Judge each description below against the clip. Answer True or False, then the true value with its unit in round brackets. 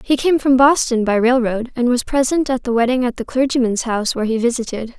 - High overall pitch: True (245 Hz)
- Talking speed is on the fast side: True (230 wpm)